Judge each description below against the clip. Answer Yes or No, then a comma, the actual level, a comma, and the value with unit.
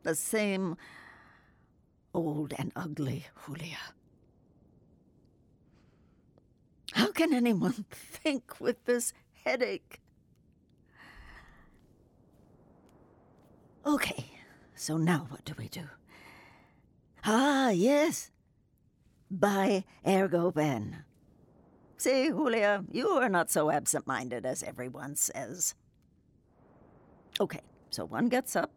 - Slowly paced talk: Yes, slow, 85 wpm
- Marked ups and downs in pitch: Yes, wide, 8.8 semitones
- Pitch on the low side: No, medium, 175 Hz